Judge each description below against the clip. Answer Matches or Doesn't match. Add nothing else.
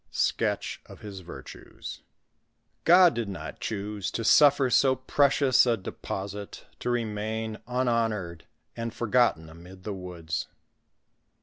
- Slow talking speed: Matches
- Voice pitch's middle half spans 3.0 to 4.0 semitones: Doesn't match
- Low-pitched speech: Matches